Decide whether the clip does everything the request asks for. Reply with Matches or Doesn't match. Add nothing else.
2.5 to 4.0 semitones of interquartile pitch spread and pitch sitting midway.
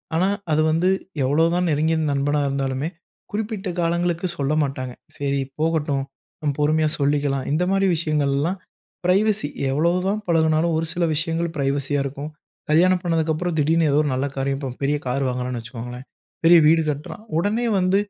Matches